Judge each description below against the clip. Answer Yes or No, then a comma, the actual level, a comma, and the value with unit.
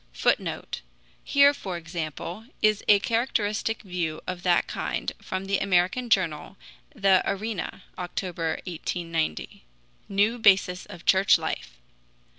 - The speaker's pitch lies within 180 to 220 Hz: Yes, high, 190 Hz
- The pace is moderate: No, slow, 115 wpm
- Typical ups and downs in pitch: Yes, average, 3.2 semitones